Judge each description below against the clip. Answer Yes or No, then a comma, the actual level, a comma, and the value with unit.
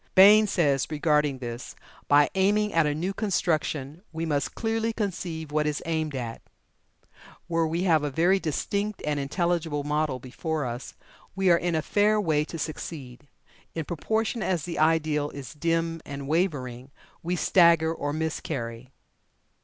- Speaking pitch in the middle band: Yes, medium, 160 Hz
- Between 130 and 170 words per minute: Yes, average, 155 wpm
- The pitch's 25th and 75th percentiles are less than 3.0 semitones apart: No, average, 3.4 semitones